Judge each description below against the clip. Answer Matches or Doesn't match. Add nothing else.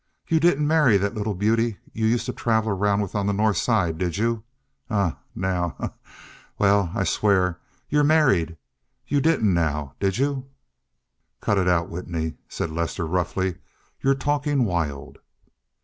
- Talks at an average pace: Matches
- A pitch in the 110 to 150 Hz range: Doesn't match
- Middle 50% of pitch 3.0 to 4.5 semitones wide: Doesn't match